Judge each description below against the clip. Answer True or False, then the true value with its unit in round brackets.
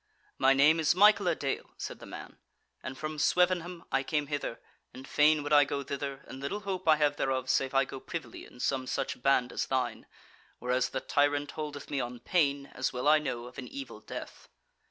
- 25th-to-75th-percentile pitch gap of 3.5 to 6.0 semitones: False (2.7 semitones)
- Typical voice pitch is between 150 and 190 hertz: False (140 Hz)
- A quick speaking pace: True (210 wpm)